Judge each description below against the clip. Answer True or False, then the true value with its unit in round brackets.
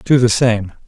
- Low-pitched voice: True (115 Hz)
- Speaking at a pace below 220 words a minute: True (205 wpm)